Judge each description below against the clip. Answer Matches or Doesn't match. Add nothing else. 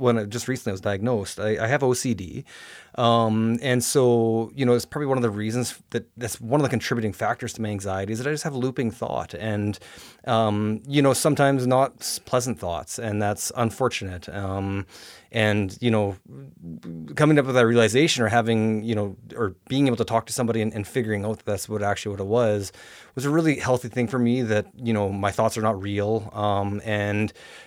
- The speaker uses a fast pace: Matches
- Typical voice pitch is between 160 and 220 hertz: Doesn't match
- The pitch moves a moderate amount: Matches